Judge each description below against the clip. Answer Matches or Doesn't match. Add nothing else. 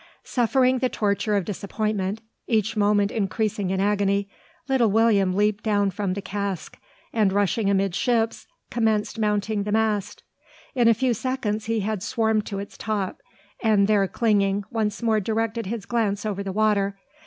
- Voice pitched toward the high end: Matches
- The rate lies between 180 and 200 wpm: Doesn't match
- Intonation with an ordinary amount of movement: Doesn't match